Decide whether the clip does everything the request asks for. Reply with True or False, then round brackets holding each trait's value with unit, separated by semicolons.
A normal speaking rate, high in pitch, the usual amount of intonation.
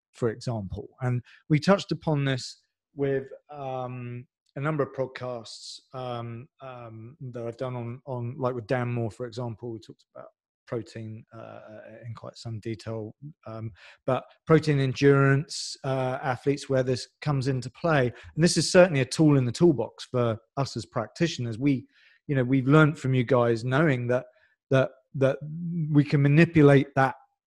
False (165 wpm; 130 Hz; 3.2 semitones)